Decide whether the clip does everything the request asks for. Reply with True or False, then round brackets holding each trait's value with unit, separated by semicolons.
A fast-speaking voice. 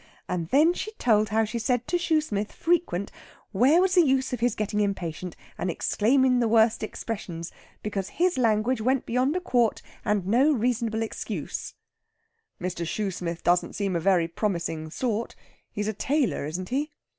False (165 wpm)